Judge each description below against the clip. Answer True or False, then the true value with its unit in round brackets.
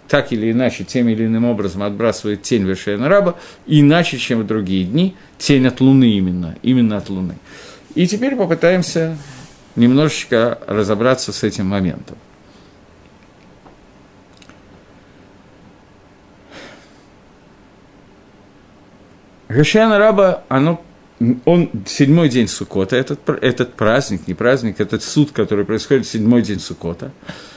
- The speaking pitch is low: True (120 Hz)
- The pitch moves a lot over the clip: True (6.3 semitones)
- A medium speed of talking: False (105 wpm)